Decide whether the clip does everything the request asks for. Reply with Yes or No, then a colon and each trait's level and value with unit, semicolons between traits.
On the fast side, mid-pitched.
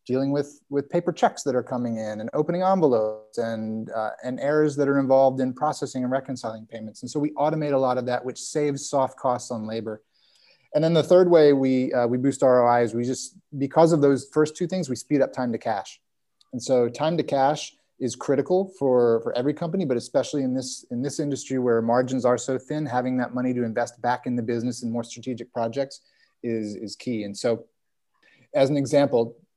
No: fast, 215 wpm; low, 130 Hz